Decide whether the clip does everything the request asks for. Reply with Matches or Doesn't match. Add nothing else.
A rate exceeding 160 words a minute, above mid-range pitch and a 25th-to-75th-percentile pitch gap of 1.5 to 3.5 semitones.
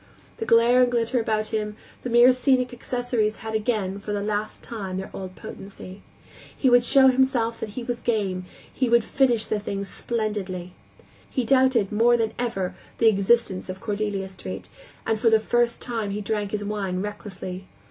Matches